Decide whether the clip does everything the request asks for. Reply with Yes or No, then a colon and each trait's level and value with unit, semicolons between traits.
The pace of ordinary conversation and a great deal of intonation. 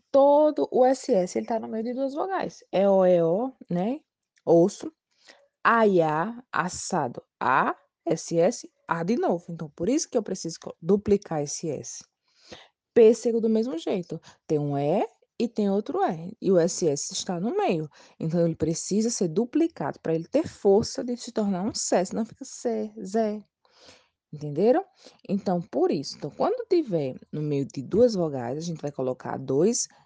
Yes: average, 170 wpm; wide, 7.0 semitones